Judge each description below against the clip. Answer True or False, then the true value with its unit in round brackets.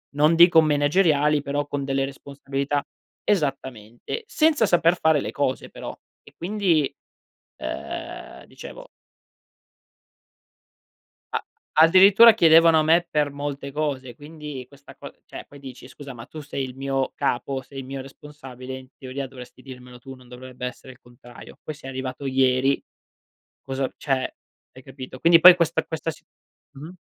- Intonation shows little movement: False (3.1 semitones)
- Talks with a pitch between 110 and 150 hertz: True (140 Hz)